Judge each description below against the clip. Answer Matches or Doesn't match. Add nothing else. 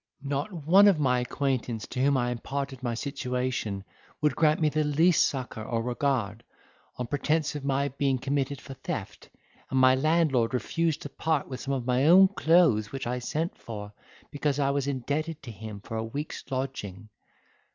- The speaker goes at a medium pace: Matches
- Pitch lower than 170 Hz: Matches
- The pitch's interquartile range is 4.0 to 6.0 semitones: Doesn't match